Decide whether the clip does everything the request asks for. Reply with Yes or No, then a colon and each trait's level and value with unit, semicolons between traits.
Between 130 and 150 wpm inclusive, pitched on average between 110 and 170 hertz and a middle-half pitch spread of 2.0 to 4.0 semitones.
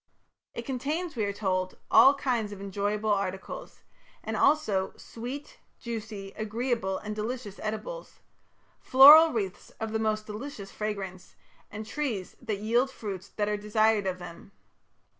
No: average, 140 wpm; high, 215 Hz; average, 3.7 semitones